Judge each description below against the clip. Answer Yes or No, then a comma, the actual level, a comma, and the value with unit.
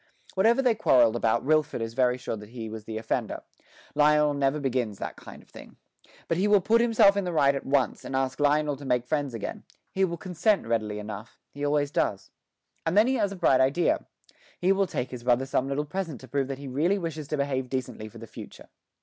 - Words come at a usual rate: No, fast, 225 wpm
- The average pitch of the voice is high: No, medium, 140 Hz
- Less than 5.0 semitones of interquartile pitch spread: No, wide, 5.4 semitones